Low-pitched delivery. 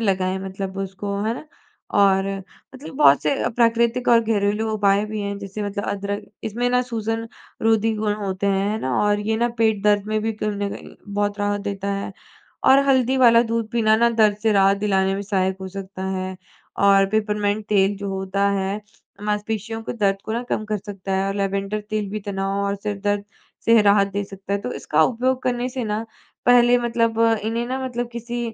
No: high, 210 Hz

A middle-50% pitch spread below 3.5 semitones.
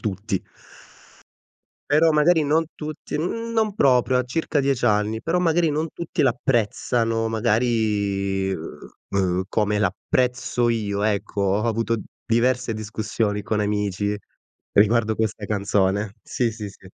No: average, 4.0 semitones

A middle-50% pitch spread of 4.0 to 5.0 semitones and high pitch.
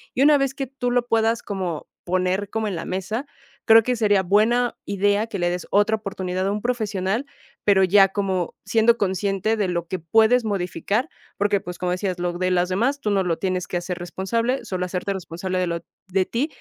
No: average, 3.4 semitones; high, 195 Hz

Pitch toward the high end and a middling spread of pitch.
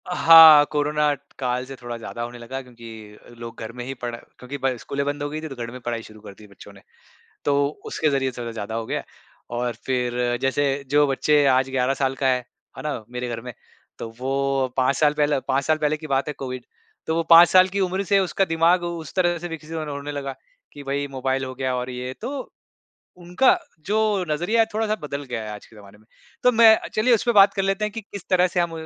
No: medium, 140 Hz; average, 4.8 semitones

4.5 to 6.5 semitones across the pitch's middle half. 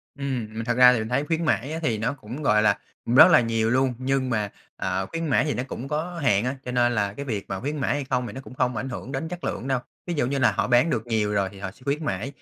No: average, 4.1 semitones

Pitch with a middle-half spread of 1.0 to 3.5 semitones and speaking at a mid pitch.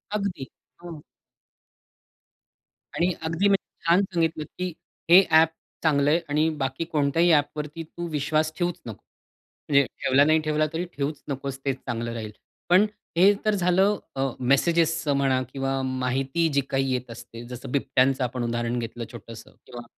No: average, 4.2 semitones; medium, 145 Hz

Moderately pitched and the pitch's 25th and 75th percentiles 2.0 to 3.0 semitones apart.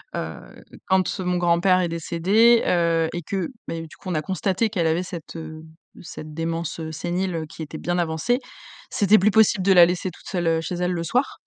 Yes: medium, 175 Hz; narrow, 2.4 semitones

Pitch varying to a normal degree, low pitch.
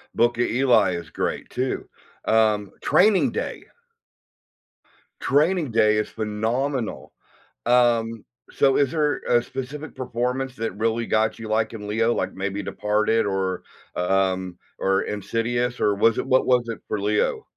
Yes: average, 3.1 semitones; low, 115 Hz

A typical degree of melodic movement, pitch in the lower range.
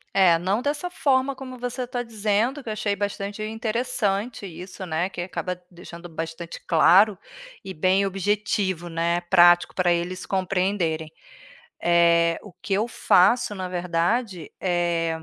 No: average, 3.7 semitones; high, 190 Hz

